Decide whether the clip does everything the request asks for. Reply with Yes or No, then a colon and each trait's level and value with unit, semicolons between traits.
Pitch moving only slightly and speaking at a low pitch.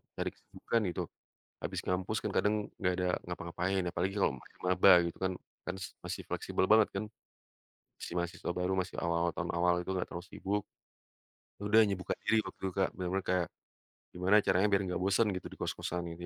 Yes: narrow, 1.6 semitones; very low, 90 Hz